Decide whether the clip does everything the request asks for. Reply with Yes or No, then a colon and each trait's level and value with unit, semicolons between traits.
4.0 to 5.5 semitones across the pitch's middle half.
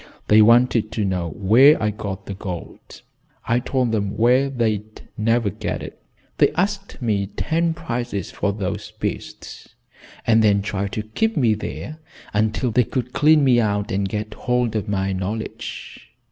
No: average, 3.4 semitones